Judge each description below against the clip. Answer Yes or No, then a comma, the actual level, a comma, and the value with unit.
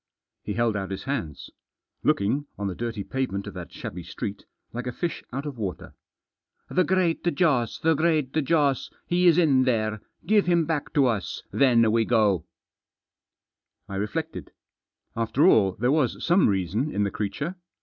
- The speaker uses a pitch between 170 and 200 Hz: No, low, 125 Hz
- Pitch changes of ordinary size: No, wide, 7.0 semitones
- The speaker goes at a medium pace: Yes, average, 170 wpm